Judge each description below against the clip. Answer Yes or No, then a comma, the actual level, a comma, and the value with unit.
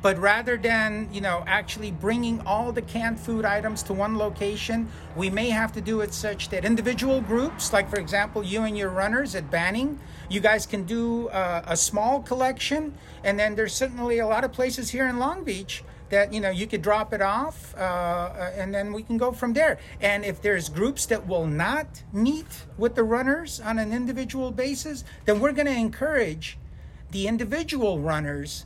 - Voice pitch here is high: Yes, high, 220 Hz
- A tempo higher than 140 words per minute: Yes, average, 195 wpm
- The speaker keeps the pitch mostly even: No, average, 3.5 semitones